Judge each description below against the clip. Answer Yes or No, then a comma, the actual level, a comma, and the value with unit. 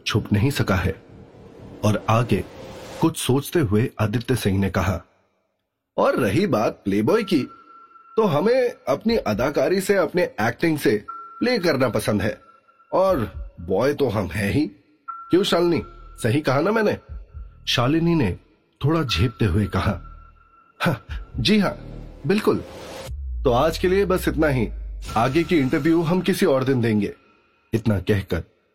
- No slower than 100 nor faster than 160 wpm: Yes, average, 145 wpm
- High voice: No, low, 130 Hz